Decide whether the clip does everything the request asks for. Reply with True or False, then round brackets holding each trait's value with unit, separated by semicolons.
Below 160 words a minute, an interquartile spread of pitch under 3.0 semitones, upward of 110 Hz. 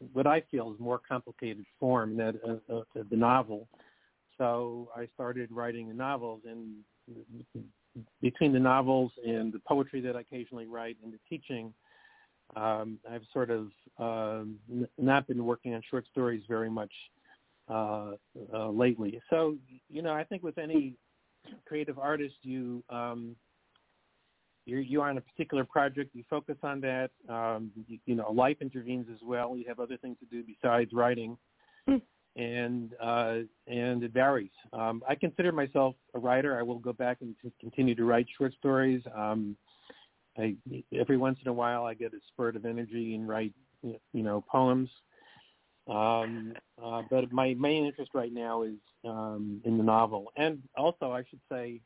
False (170 wpm; 2.4 semitones; 120 Hz)